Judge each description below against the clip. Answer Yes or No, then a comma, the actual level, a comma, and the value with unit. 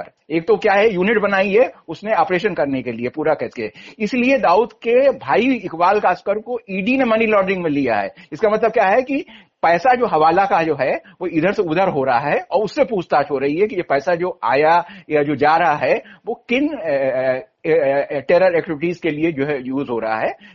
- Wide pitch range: Yes, wide, 6.3 semitones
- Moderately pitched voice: Yes, medium, 180 Hz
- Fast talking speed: Yes, fast, 215 wpm